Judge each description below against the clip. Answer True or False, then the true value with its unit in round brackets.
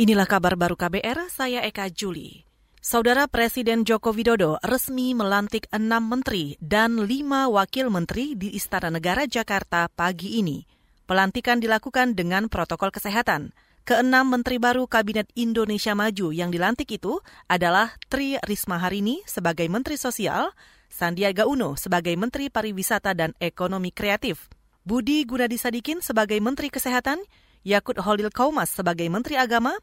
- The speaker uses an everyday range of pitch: True (4.5 semitones)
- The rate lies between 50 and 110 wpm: False (130 wpm)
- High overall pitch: True (220 Hz)